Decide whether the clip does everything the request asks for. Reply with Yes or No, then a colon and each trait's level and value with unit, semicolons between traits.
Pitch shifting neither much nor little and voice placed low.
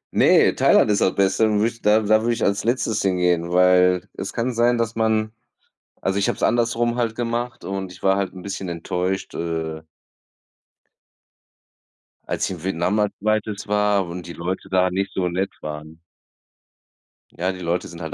Yes: average, 3.3 semitones; very low, 95 Hz